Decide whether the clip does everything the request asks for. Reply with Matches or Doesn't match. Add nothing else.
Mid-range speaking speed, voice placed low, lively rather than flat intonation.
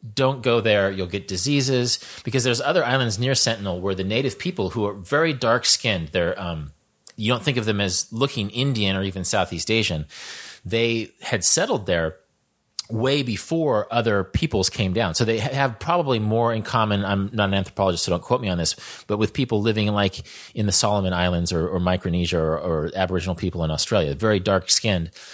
Doesn't match